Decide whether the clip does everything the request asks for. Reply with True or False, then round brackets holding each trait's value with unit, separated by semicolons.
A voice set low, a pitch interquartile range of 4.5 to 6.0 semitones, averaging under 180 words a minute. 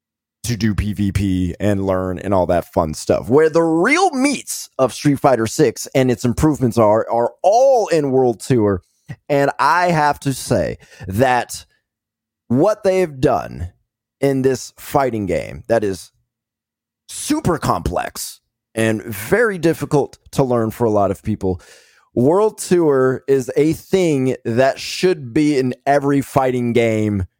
True (125 Hz; 5.4 semitones; 145 wpm)